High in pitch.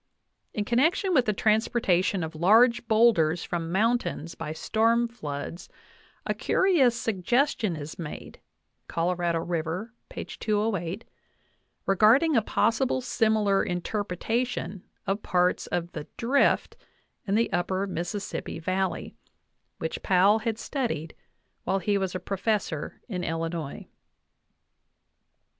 Yes: high, 200 Hz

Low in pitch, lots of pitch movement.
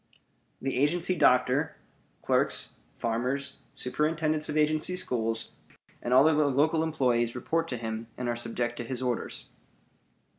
No: low, 130 Hz; average, 4.3 semitones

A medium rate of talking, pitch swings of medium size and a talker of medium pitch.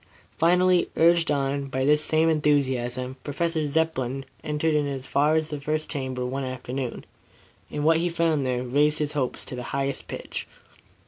Yes: average, 170 wpm; average, 3.1 semitones; medium, 145 Hz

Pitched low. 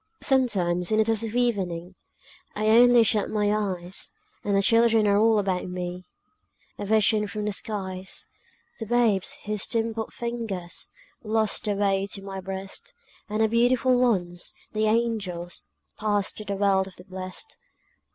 No: high, 210 Hz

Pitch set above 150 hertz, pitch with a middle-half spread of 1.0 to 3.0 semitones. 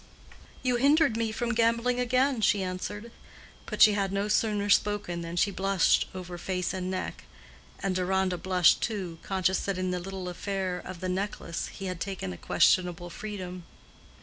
Yes: high, 190 Hz; narrow, 2.5 semitones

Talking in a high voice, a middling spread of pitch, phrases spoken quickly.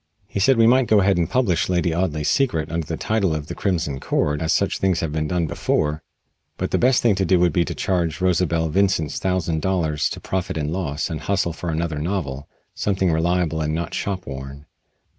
No: very low, 85 Hz; average, 3.5 semitones; fast, 215 wpm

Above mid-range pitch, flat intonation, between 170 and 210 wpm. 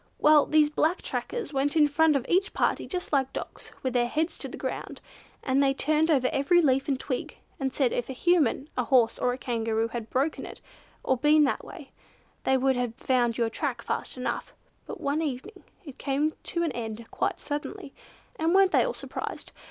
No: very high, 275 Hz; average, 3.7 semitones; fast, 205 wpm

